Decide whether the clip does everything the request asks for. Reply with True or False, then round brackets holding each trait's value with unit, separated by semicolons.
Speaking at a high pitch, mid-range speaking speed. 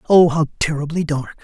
False (155 Hz; 165 wpm)